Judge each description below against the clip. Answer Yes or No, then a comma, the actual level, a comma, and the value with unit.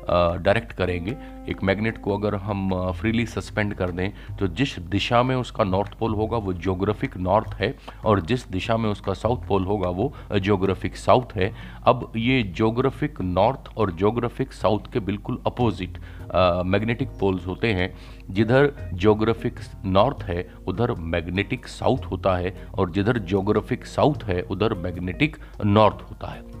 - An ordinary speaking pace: Yes, average, 160 wpm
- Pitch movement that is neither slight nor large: Yes, average, 3.9 semitones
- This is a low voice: Yes, low, 105 Hz